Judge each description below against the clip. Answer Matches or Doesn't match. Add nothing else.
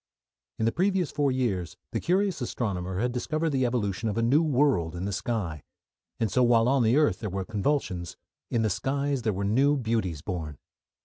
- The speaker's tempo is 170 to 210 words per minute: Matches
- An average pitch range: Doesn't match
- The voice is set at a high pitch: Doesn't match